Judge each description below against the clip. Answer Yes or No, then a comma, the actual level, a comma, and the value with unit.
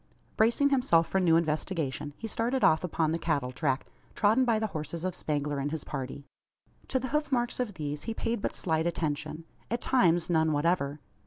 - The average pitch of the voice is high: No, medium, 165 Hz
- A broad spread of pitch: Yes, wide, 6.9 semitones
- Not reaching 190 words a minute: No, average, 195 wpm